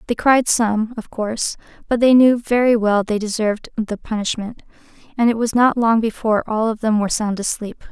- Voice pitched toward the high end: Yes, high, 225 Hz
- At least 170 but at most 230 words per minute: Yes, average, 195 wpm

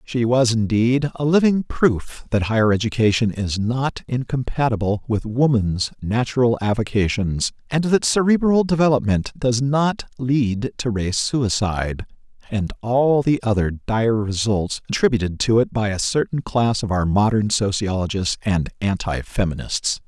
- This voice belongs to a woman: No, male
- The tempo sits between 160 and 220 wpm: No, average, 140 wpm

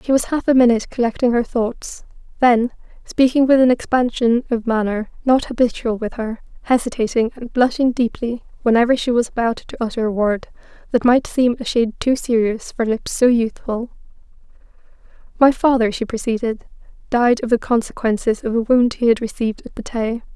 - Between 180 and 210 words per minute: No, average, 170 wpm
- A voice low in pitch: No, high, 235 Hz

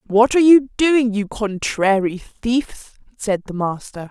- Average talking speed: Yes, average, 145 wpm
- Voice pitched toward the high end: Yes, high, 225 Hz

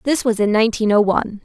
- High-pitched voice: Yes, high, 220 Hz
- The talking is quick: Yes, fast, 250 wpm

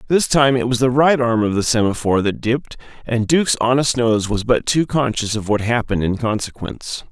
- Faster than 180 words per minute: Yes, average, 200 wpm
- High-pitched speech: No, low, 120 Hz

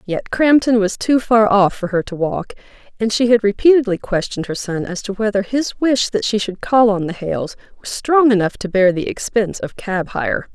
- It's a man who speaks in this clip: No, female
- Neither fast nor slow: No, fast, 220 wpm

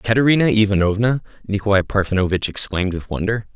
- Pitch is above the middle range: No, low, 105 Hz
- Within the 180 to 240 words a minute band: No, slow, 120 wpm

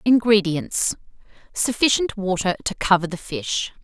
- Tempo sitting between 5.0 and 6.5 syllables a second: No, 4.5 syllables/s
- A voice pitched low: No, high, 200 Hz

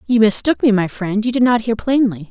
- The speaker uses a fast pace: Yes, fast, 260 wpm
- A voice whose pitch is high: Yes, high, 225 Hz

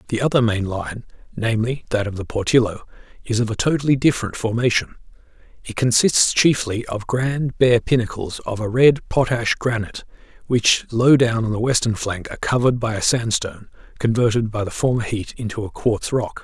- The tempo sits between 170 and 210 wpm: Yes, average, 175 wpm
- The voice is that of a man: Yes, male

